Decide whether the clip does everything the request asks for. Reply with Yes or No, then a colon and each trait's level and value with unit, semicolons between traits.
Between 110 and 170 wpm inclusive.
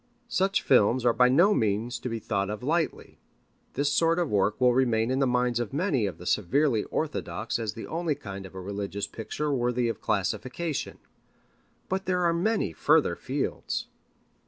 No: average, 180 wpm